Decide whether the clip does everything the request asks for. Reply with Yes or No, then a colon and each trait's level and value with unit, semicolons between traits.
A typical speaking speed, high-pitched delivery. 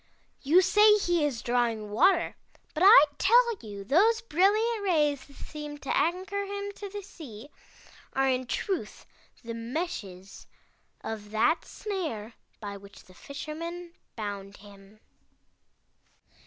No: slow, 130 wpm; very high, 295 Hz